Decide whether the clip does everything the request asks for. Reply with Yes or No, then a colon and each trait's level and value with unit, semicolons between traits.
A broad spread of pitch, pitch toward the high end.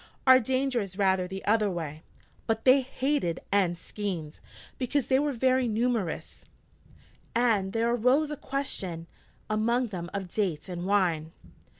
Yes: wide, 5.8 semitones; high, 215 Hz